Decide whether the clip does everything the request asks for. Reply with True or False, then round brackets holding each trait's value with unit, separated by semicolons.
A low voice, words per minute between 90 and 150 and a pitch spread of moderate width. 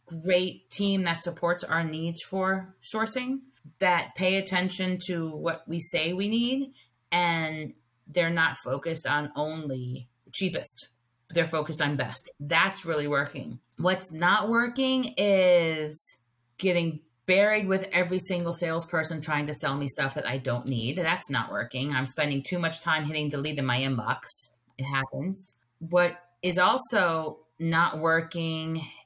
False (165 Hz; 145 wpm; 4.1 semitones)